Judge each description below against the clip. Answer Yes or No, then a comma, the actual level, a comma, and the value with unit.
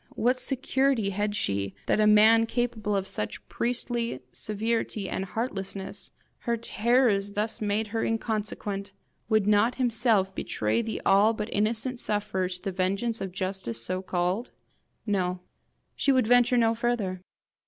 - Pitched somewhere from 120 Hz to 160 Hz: No, high, 210 Hz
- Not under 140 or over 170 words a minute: Yes, average, 145 wpm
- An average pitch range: Yes, average, 3.3 semitones